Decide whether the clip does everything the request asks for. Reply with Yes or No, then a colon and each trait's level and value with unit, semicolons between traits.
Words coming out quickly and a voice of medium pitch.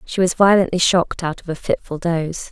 Yes: fast, 215 wpm; medium, 175 Hz